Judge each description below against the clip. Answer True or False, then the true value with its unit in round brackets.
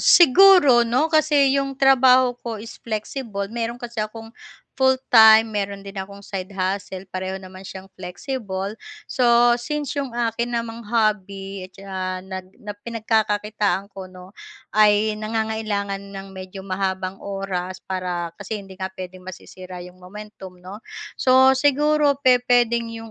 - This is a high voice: True (210 Hz)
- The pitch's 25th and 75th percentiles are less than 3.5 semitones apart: False (4.0 semitones)